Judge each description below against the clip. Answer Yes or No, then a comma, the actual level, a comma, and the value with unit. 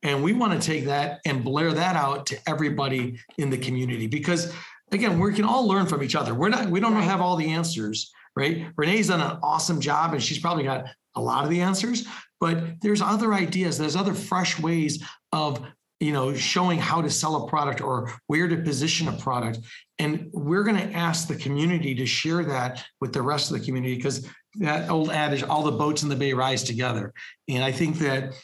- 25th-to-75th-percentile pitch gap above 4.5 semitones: No, average, 4.2 semitones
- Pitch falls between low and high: Yes, medium, 155 Hz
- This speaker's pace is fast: Yes, fast, 215 wpm